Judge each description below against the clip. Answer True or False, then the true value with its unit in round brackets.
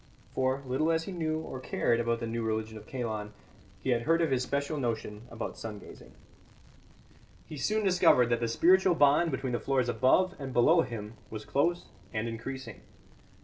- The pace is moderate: True (185 wpm)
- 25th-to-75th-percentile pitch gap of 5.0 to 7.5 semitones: True (5.3 semitones)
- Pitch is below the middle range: True (130 Hz)